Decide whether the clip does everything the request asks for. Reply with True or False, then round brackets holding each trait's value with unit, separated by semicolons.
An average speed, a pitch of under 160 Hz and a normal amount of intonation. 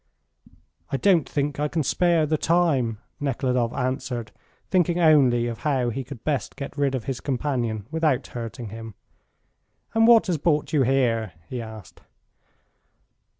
True (150 wpm; 135 Hz; 4.5 semitones)